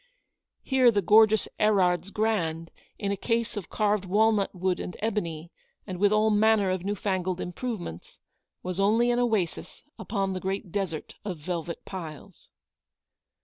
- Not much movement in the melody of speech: No, average, 3.1 semitones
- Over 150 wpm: No, average, 145 wpm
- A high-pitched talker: Yes, high, 195 Hz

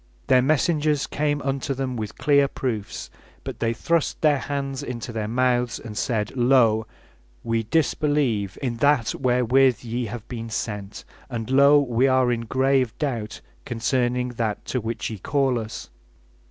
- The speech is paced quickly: No, average, 155 wpm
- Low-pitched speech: Yes, low, 125 Hz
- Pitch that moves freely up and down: No, average, 3.2 semitones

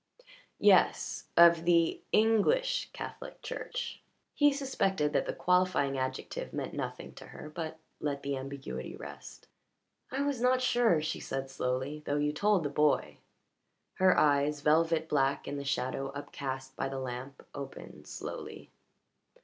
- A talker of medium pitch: Yes, medium, 150 Hz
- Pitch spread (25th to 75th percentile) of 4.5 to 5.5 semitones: Yes, average, 5.1 semitones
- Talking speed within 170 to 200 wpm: No, average, 140 wpm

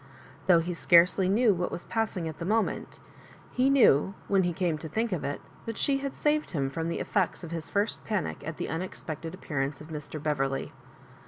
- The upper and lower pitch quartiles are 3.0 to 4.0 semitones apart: No, average, 4.8 semitones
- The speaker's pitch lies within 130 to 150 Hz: No, medium, 175 Hz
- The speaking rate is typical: No, fast, 210 wpm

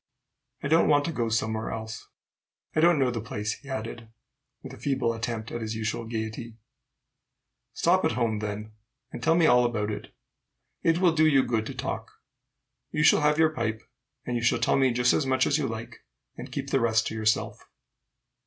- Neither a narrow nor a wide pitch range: Yes, average, 4.1 semitones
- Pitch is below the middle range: Yes, low, 120 Hz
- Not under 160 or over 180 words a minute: No, average, 200 wpm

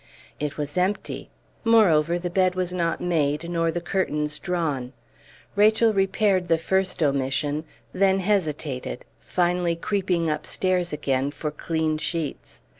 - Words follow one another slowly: Yes, slow, 125 wpm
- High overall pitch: No, medium, 170 Hz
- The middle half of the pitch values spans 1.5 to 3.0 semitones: No, average, 3.5 semitones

